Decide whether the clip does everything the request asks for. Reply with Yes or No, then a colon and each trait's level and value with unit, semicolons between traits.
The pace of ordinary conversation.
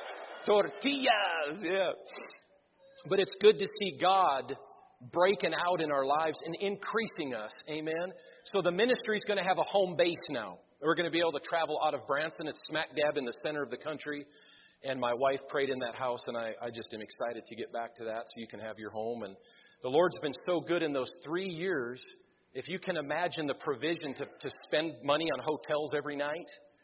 No: fast, 210 wpm